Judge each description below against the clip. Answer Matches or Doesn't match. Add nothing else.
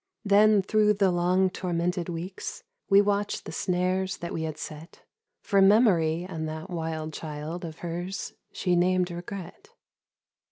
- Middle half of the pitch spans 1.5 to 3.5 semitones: Matches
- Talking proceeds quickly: Doesn't match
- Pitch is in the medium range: Matches